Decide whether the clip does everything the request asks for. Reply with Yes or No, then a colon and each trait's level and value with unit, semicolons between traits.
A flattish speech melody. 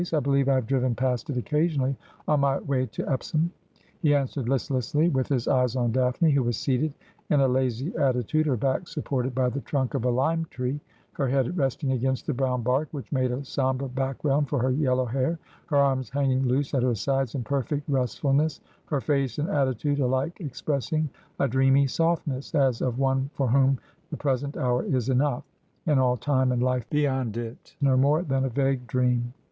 Yes: narrow, 1.9 semitones